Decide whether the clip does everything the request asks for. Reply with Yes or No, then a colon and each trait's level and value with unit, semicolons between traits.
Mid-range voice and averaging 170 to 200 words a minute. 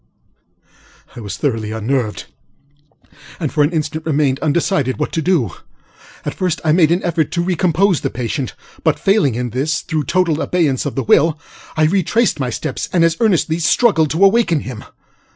Yes: medium, 155 Hz; average, 175 wpm